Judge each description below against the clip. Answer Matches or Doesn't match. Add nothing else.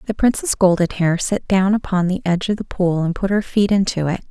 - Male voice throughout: Doesn't match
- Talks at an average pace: Doesn't match